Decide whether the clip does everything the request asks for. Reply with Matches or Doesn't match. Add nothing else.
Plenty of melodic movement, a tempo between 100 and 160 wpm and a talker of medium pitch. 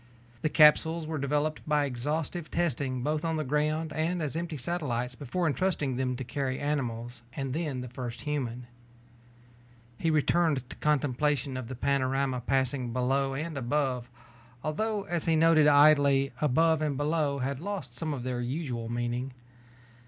Doesn't match